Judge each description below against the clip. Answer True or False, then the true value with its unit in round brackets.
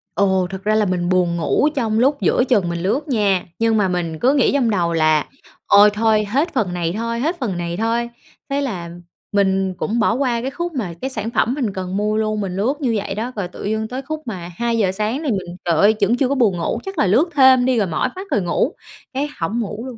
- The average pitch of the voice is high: True (215 Hz)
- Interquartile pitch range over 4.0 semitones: True (5.0 semitones)